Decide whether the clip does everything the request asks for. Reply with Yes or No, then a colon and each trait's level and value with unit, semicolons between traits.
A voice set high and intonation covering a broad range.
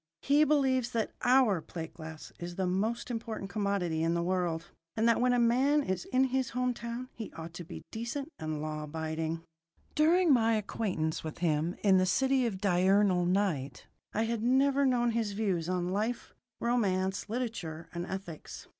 Yes: high, 205 Hz; wide, 5.9 semitones